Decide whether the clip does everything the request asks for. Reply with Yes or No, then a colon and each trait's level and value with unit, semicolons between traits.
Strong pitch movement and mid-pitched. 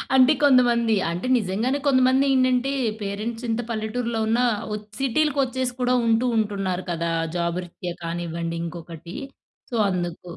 No: wide, 6.2 semitones; high, 225 Hz